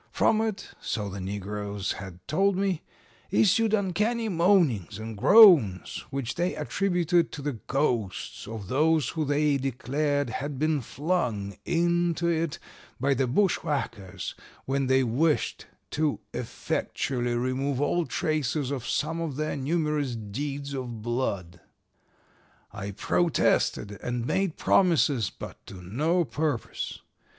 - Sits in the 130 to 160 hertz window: Yes, medium, 140 Hz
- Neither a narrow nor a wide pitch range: No, wide, 6.3 semitones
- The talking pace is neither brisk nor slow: No, slow, 125 wpm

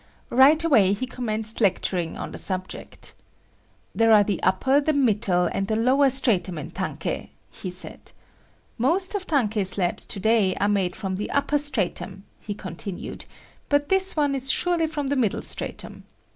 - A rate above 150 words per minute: Yes, average, 165 wpm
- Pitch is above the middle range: Yes, high, 220 Hz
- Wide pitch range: Yes, wide, 6.6 semitones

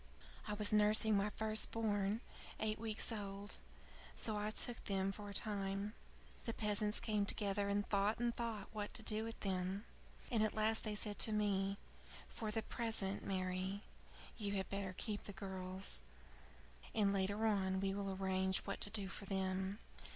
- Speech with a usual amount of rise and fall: No, narrow, 1.7 semitones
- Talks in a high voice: Yes, high, 205 Hz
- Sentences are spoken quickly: No, average, 170 wpm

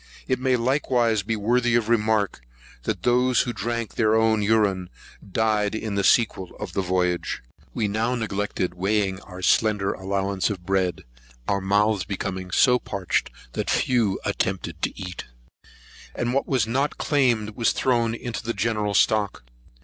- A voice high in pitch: No, low, 105 Hz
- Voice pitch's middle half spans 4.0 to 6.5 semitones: No, average, 3.3 semitones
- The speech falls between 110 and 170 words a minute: Yes, average, 155 wpm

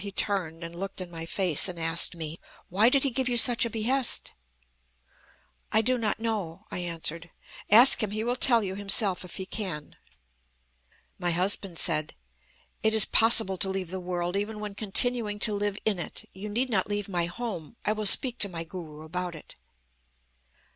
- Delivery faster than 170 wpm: Yes, average, 190 wpm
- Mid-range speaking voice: No, high, 195 Hz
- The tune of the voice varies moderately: Yes, average, 4.1 semitones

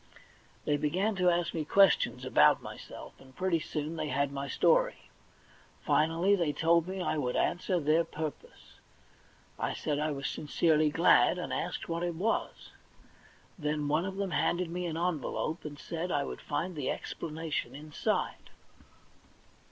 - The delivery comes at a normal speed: Yes, average, 155 wpm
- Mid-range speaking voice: Yes, medium, 165 Hz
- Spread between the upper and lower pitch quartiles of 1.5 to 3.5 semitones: Yes, average, 3.0 semitones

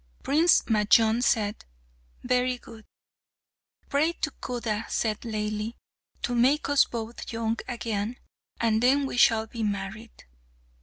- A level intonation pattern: Yes, narrow, 2.3 semitones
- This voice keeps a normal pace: No, slow, 120 wpm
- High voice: Yes, high, 230 Hz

